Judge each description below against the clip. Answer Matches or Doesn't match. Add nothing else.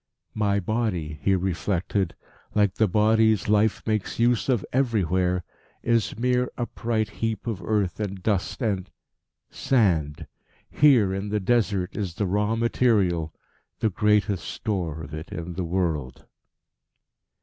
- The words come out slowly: Matches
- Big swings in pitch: Doesn't match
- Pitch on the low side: Matches